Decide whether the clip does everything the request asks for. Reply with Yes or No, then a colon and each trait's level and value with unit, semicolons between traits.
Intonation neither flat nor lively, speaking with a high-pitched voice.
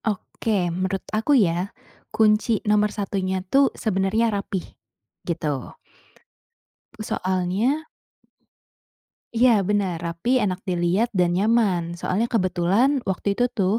Yes: average, 3.3 semitones; high, 195 Hz